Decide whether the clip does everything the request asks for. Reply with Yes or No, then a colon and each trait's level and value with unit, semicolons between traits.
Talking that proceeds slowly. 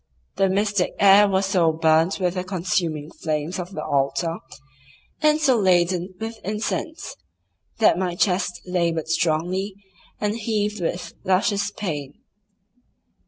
Yes: slow, 125 wpm